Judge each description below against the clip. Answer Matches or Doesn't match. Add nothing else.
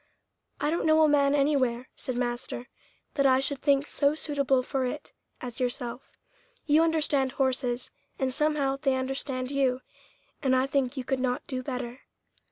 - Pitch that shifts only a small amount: Matches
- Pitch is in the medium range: Doesn't match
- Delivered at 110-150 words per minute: Doesn't match